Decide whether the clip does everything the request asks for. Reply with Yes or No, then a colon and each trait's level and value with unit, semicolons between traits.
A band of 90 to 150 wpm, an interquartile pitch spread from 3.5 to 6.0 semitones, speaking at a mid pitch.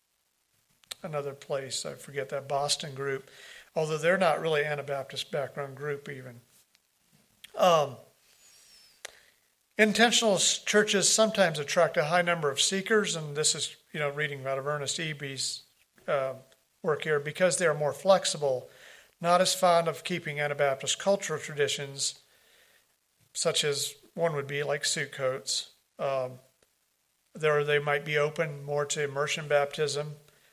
No: slow, 135 wpm; average, 2.9 semitones; medium, 145 Hz